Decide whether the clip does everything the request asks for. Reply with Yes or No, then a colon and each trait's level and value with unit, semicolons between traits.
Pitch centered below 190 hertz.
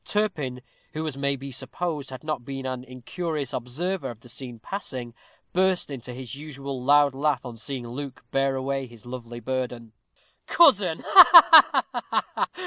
Yes: low, 135 Hz